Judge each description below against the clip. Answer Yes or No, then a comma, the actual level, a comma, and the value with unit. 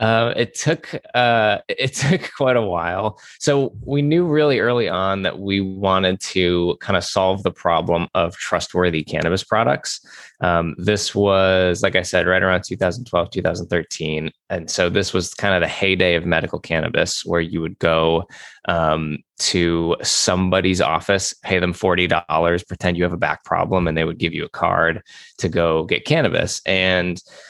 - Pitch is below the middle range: Yes, very low, 90 Hz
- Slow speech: No, average, 170 wpm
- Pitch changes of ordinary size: No, narrow, 2.3 semitones